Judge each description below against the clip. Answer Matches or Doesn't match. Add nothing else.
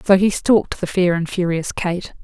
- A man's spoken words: Doesn't match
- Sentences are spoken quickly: Matches